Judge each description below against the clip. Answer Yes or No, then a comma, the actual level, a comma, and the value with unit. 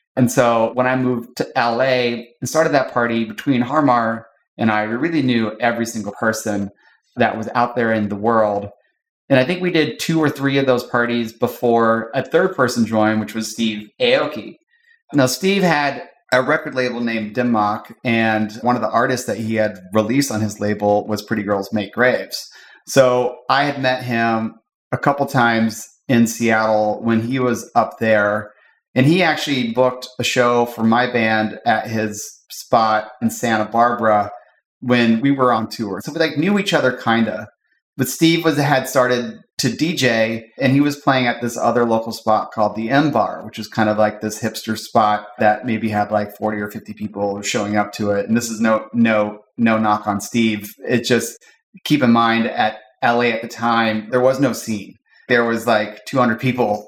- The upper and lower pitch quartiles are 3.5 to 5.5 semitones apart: No, average, 2.7 semitones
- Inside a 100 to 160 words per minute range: No, average, 195 wpm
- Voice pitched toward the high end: No, low, 115 Hz